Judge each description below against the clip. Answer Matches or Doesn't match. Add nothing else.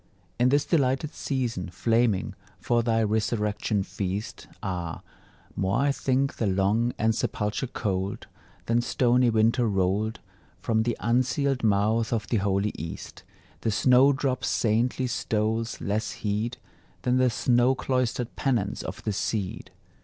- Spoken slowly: Matches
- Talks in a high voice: Doesn't match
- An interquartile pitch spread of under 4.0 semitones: Matches